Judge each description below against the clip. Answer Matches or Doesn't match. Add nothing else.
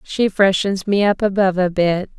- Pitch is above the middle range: Matches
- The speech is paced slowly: Doesn't match